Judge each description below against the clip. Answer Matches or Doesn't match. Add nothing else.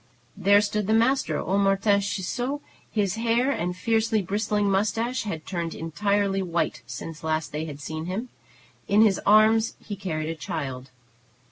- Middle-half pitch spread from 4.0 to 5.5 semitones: Matches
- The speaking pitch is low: Doesn't match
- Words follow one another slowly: Doesn't match